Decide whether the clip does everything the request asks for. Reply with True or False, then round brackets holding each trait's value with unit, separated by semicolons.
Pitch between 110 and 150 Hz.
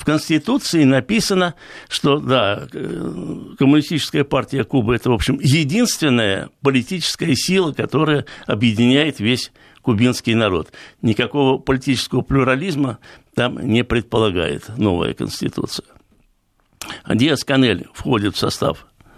True (135 Hz)